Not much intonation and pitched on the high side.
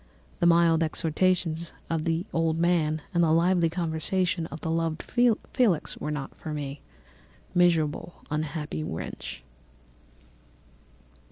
No: narrow, 1.8 semitones; medium, 165 Hz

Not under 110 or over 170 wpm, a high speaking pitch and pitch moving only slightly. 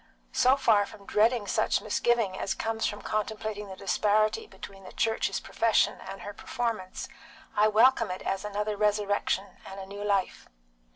Yes: average, 160 wpm; high, 210 Hz; narrow, 2.0 semitones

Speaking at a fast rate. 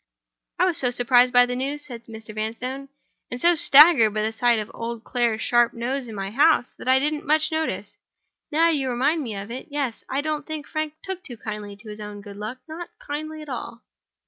Yes: fast, 210 wpm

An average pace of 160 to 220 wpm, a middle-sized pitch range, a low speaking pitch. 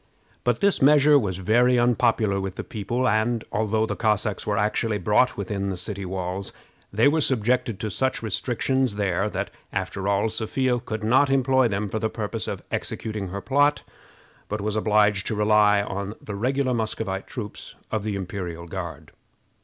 Yes: average, 170 wpm; average, 3.4 semitones; low, 110 Hz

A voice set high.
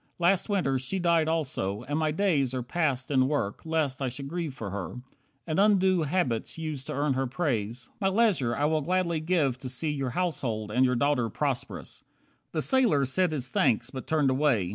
No: medium, 145 Hz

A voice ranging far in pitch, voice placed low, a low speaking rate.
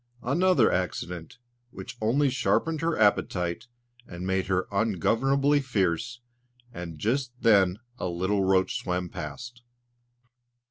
Yes: wide, 5.8 semitones; low, 105 Hz; slow, 110 wpm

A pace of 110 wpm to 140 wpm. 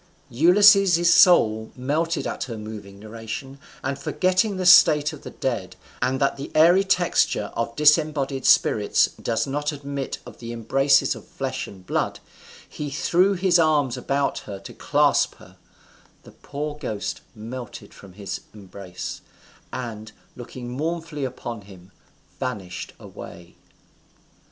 Yes: slow, 135 wpm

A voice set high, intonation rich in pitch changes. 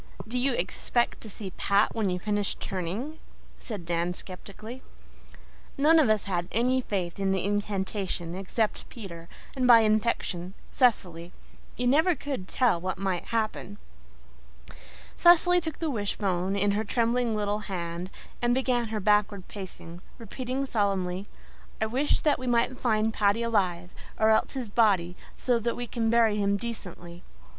No: high, 210 Hz; average, 4.2 semitones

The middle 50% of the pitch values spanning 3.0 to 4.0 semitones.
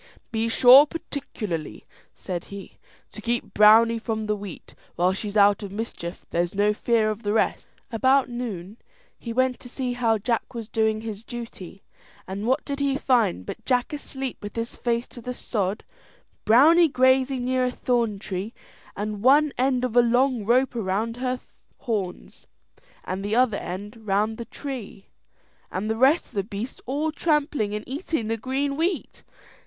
Yes: average, 3.7 semitones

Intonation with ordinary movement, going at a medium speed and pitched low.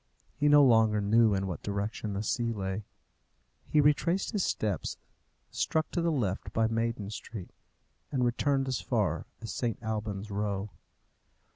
Yes: average, 4.5 semitones; average, 150 wpm; low, 110 Hz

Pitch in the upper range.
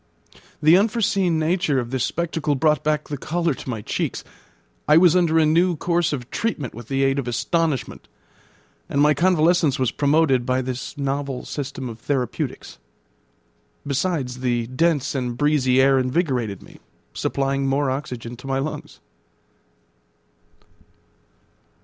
No: medium, 140 Hz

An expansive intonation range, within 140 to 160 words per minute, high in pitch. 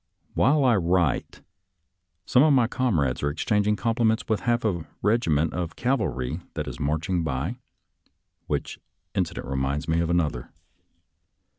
No: wide, 7.7 semitones; average, 145 wpm; very low, 85 Hz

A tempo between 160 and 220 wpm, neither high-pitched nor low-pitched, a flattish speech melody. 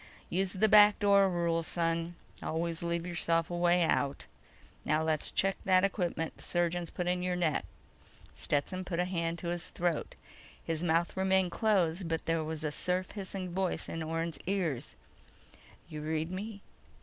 Yes: average, 165 wpm; medium, 175 Hz; narrow, 2.2 semitones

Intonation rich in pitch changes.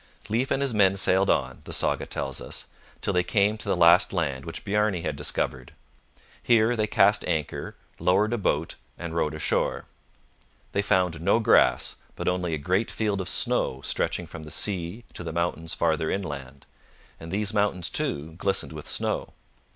No: average, 4.2 semitones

